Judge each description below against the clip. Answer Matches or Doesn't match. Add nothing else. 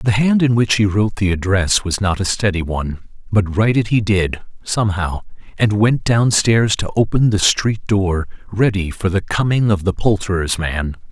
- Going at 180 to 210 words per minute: Matches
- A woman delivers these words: Doesn't match